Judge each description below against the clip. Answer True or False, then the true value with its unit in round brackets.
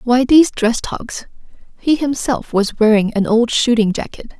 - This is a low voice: False (240 Hz)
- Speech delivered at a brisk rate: False (165 wpm)